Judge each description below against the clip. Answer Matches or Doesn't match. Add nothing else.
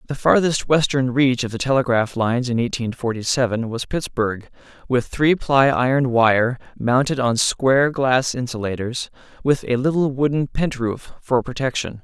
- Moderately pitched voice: Doesn't match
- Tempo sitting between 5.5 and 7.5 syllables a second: Doesn't match